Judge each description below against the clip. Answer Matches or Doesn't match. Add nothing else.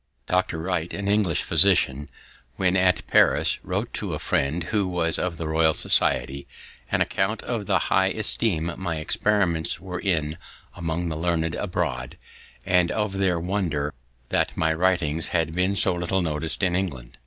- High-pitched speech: Doesn't match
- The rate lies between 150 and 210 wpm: Matches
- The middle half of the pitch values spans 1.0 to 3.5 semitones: Matches